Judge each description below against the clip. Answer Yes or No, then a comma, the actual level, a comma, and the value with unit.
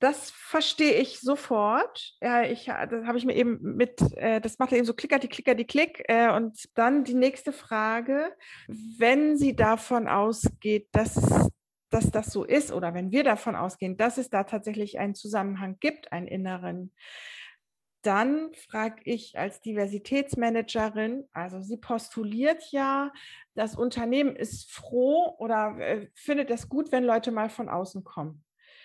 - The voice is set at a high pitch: Yes, high, 235 Hz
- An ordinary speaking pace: Yes, average, 150 wpm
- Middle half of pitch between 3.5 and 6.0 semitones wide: Yes, average, 4.2 semitones